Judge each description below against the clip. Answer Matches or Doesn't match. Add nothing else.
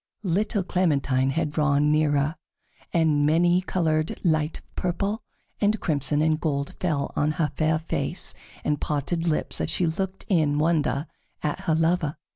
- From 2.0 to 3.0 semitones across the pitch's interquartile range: Matches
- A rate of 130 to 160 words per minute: Matches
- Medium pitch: Matches